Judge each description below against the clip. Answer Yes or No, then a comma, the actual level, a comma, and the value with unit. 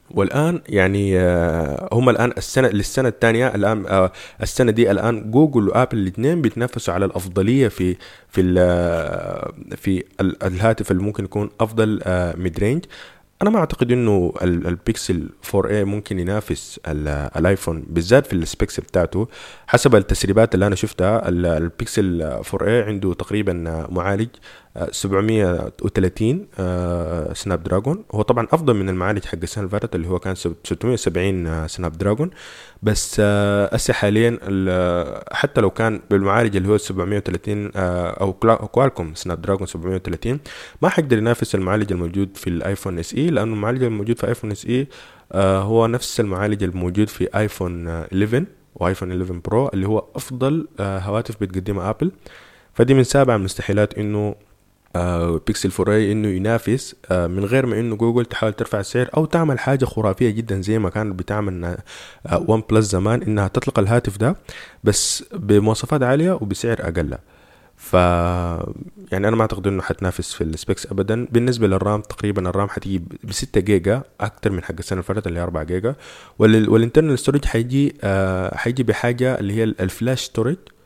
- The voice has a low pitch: Yes, low, 105 Hz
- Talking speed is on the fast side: Yes, fast, 145 wpm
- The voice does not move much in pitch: No, average, 4.0 semitones